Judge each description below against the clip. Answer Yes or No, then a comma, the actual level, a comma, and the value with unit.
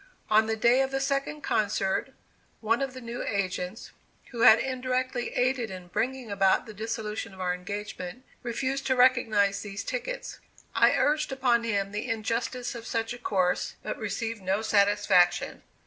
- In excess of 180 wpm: No, average, 165 wpm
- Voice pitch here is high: Yes, high, 225 Hz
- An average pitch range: Yes, average, 4.0 semitones